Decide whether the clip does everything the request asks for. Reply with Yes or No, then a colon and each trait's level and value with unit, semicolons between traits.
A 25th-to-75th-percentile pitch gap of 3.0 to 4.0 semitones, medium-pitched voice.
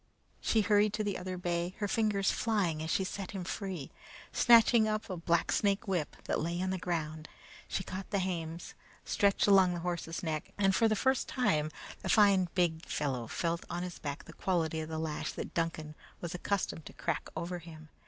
Yes: average, 3.6 semitones; medium, 180 Hz